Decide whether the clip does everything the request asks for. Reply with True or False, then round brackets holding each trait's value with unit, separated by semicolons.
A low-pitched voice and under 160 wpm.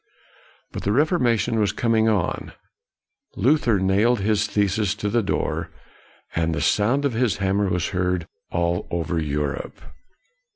True (100 Hz; 135 wpm)